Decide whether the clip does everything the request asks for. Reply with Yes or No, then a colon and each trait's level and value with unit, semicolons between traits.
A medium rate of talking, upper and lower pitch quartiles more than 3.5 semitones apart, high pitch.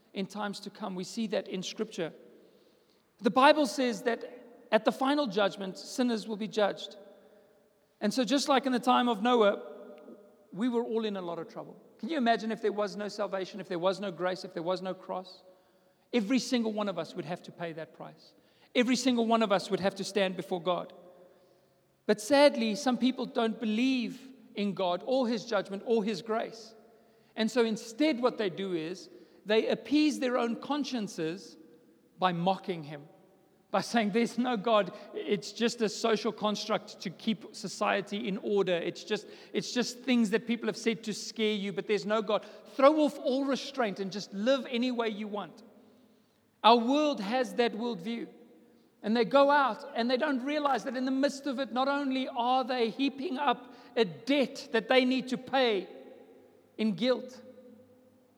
Yes: average, 190 wpm; average, 4.1 semitones; high, 220 Hz